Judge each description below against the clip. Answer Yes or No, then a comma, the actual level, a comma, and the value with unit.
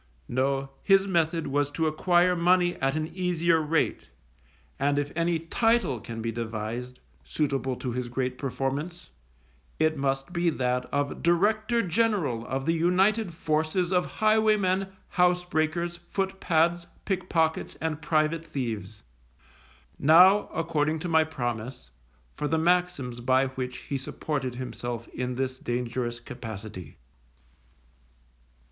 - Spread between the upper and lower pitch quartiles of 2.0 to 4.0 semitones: No, wide, 5.5 semitones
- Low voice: No, medium, 155 Hz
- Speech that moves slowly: Yes, slow, 125 wpm